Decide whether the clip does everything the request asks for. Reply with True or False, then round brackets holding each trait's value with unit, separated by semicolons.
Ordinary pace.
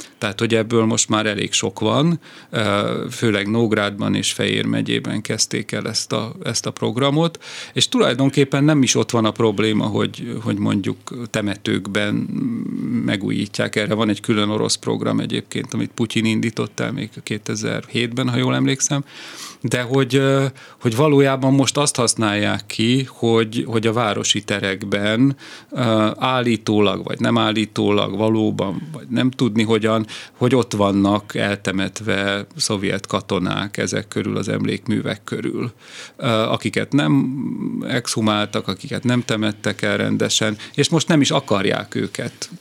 True (135 wpm)